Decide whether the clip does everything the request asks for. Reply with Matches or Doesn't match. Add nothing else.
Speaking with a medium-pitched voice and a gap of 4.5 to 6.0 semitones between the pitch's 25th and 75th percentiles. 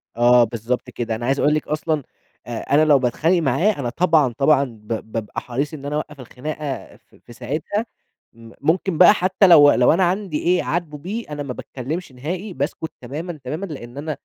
Matches